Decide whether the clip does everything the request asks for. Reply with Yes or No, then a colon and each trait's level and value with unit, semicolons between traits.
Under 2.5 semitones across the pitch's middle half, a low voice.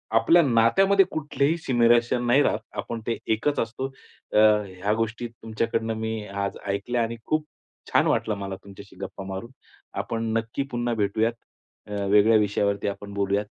No: average, 2.8 semitones; low, 115 Hz